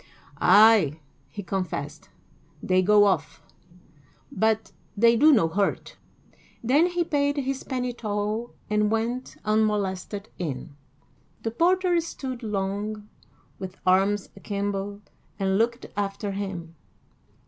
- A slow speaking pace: Yes, slow, 110 wpm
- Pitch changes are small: No, average, 3.4 semitones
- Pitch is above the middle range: Yes, high, 210 Hz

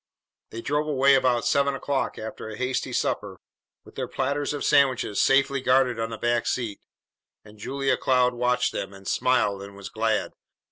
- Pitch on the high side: No, low, 125 Hz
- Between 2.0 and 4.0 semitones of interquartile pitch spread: Yes, average, 3.6 semitones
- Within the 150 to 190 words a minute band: Yes, average, 175 wpm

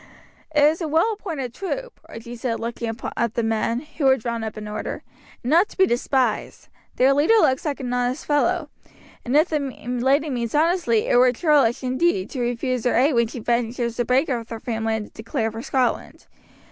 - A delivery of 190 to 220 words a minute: Yes, average, 200 wpm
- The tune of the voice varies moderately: Yes, average, 4.2 semitones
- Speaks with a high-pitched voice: Yes, very high, 250 Hz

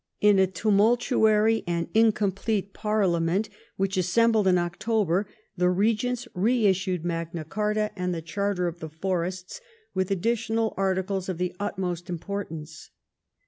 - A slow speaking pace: Yes, slow, 130 wpm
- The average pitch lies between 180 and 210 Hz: Yes, high, 190 Hz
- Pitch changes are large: No, average, 3.2 semitones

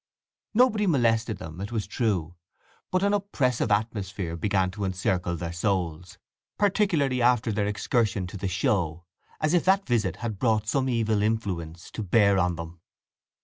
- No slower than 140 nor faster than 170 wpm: Yes, average, 155 wpm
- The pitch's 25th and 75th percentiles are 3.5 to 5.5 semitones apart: Yes, average, 5.1 semitones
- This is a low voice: Yes, low, 105 Hz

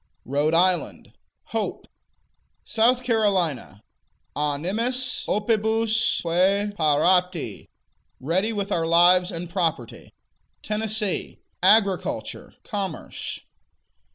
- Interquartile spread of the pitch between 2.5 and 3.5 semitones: No, average, 4.5 semitones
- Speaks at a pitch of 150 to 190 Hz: Yes, medium, 185 Hz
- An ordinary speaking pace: No, slow, 70 wpm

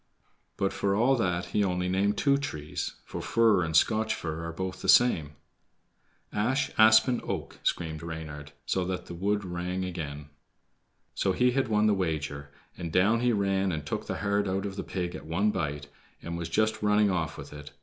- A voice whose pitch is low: Yes, very low, 95 Hz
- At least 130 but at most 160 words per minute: No, average, 190 wpm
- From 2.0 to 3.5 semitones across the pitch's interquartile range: No, average, 4.3 semitones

